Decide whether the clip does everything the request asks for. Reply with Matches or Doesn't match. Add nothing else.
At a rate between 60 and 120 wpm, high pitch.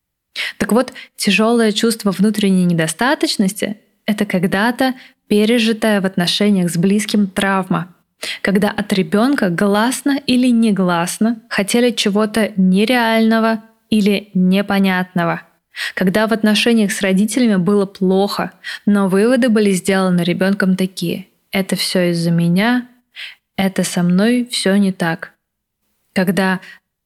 Matches